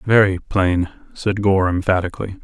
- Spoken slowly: Yes, slow, 125 wpm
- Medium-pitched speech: No, very low, 95 Hz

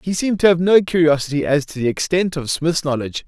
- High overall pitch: No, medium, 160 Hz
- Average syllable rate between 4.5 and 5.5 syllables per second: No, 6.3 syllables/s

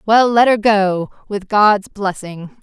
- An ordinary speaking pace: Yes, average, 160 wpm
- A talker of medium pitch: No, high, 205 Hz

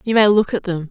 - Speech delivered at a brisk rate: Yes, fast, 330 wpm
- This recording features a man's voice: No, female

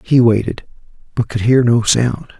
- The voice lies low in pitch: Yes, low, 120 Hz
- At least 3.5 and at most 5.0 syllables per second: Yes, 4.7 syllables/s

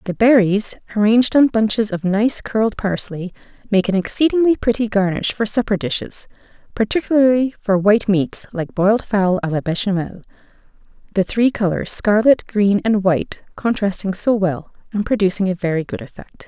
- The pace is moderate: Yes, average, 155 wpm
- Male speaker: No, female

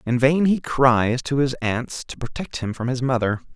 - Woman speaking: No, male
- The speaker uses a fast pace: Yes, fast, 220 wpm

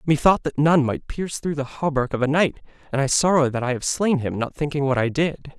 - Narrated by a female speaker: No, male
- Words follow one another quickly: Yes, fast, 260 wpm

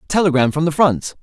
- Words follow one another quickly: No, average, 195 wpm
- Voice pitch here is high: No, medium, 150 Hz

